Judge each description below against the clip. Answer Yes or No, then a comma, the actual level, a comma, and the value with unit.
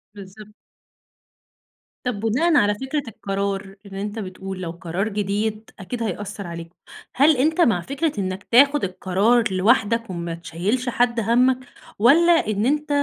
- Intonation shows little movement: No, average, 4.4 semitones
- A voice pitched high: Yes, high, 210 Hz